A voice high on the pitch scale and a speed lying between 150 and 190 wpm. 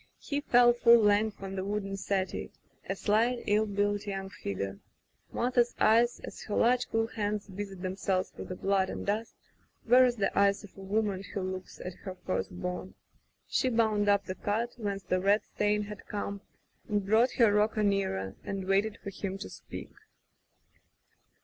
Yes: high, 205 Hz; average, 180 wpm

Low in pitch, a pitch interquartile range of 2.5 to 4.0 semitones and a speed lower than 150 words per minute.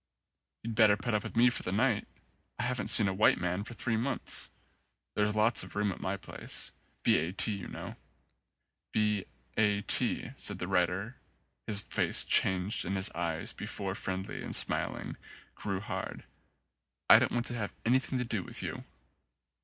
No: low, 105 Hz; average, 3.4 semitones; average, 175 wpm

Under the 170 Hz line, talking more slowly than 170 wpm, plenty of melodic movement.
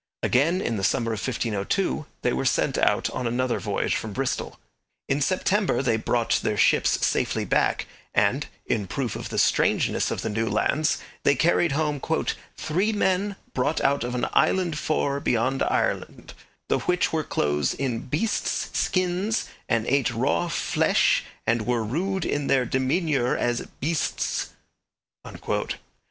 Yes: low, 135 Hz; average, 150 wpm; wide, 6.0 semitones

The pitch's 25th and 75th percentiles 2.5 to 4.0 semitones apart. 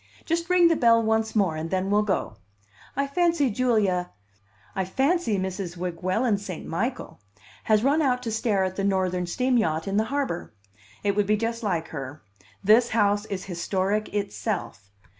No: average, 4.4 semitones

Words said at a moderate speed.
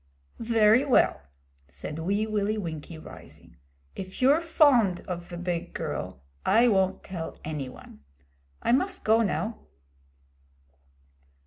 No: slow, 120 wpm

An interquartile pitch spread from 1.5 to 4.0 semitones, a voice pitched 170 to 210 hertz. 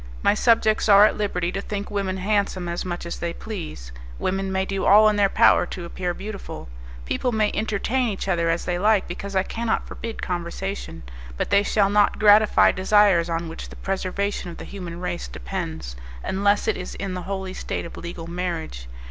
Yes: average, 3.0 semitones; high, 190 Hz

